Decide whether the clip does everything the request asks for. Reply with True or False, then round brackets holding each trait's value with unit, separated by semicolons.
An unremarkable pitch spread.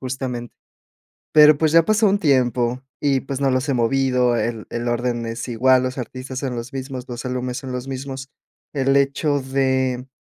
False (1.7 semitones)